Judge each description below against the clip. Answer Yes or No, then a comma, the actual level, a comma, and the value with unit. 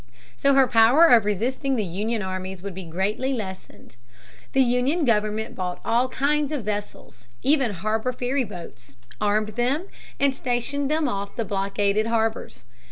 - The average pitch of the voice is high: Yes, high, 225 Hz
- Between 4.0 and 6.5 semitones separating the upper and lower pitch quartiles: Yes, average, 4.8 semitones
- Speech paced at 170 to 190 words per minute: No, average, 150 wpm